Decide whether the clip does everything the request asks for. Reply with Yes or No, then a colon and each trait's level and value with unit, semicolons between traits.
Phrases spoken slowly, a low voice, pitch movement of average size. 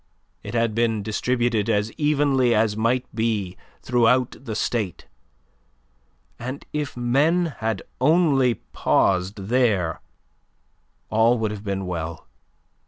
Yes: slow, 110 wpm; low, 115 Hz; average, 3.6 semitones